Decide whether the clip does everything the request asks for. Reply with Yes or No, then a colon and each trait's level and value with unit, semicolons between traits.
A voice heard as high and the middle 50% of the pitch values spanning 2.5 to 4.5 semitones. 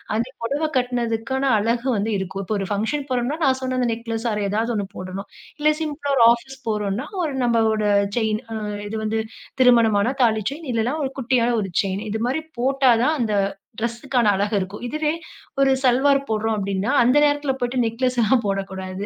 Yes: high, 235 Hz; average, 3.8 semitones